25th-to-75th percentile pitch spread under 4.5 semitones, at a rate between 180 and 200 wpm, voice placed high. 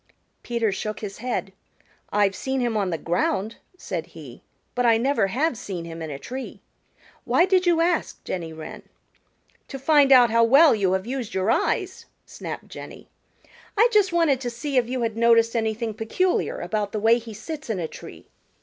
No: average, 5.1 semitones; average, 185 wpm; high, 230 Hz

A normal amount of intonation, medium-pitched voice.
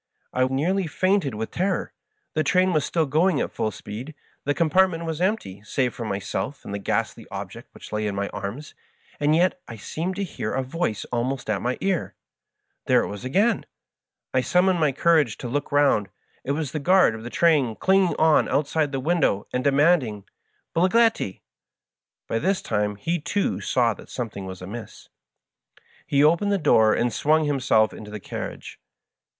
No: wide, 7.4 semitones; medium, 145 Hz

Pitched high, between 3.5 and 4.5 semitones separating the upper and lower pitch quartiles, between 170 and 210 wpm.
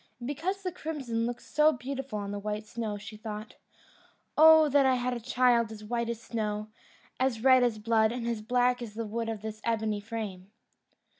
No: high, 230 Hz; average, 2.8 semitones; average, 200 wpm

